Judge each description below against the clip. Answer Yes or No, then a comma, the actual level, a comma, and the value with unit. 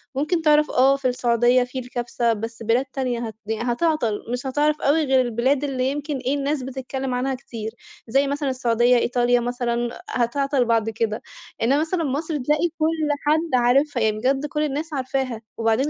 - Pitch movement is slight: No, average, 3.1 semitones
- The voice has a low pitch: No, very high, 260 Hz